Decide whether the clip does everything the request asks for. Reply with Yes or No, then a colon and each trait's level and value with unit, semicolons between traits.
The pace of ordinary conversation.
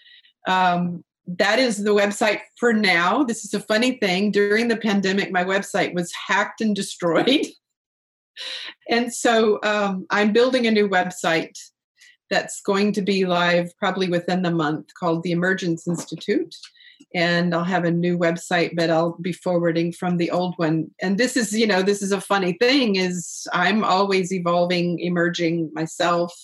Yes: average, 165 wpm